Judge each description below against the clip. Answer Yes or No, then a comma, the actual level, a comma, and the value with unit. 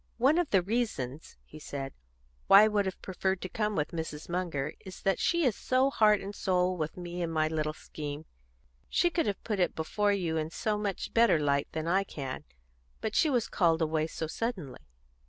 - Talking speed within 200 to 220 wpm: Yes, fast, 205 wpm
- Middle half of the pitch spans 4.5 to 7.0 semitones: Yes, average, 5.1 semitones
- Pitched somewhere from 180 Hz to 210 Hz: Yes, medium, 185 Hz